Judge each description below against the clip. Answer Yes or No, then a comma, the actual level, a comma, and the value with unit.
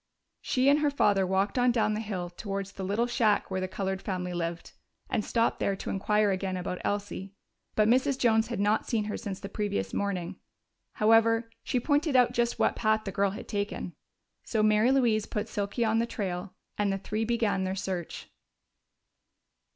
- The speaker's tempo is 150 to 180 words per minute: No, average, 190 wpm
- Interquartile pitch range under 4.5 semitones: Yes, average, 3.0 semitones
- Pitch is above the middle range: Yes, high, 210 Hz